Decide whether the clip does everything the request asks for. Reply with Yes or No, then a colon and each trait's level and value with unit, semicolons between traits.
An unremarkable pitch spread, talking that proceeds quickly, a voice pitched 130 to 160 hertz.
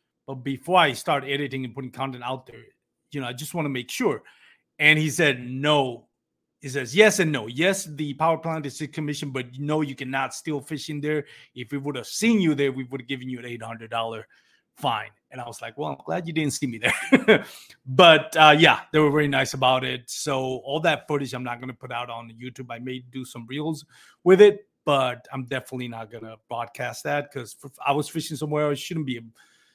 Yes: average, 3.2 semitones; fast, 230 wpm; medium, 140 Hz